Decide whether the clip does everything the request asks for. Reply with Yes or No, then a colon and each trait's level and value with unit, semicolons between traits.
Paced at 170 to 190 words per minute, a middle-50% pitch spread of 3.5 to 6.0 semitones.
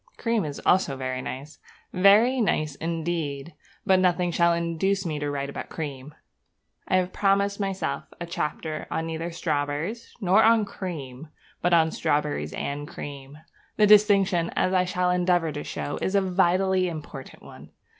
No: average, 155 wpm; average, 4.3 semitones